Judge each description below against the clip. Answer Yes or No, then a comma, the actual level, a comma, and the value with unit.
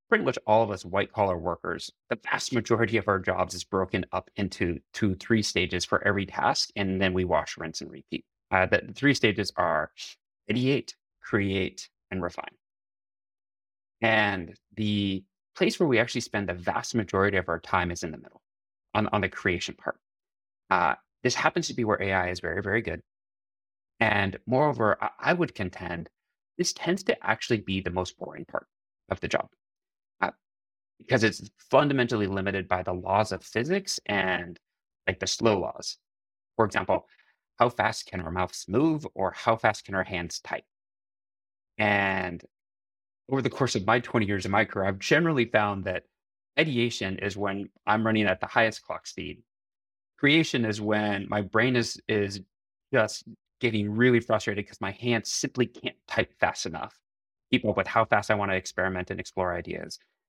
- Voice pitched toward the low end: Yes, low, 100 Hz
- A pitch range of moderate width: Yes, average, 3.4 semitones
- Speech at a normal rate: Yes, average, 175 wpm